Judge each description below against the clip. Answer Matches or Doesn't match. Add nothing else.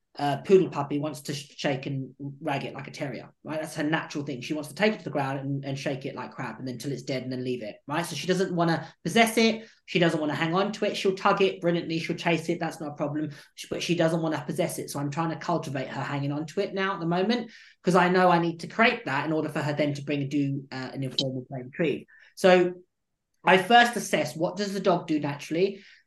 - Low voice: Doesn't match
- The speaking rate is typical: Doesn't match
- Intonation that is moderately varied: Matches